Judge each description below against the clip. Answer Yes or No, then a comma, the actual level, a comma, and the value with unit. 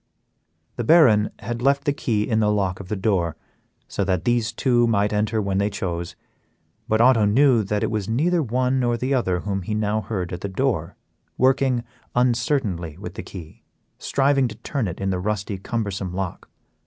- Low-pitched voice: Yes, low, 110 Hz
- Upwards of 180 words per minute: Yes, average, 190 wpm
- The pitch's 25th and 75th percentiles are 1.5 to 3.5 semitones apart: No, average, 4.1 semitones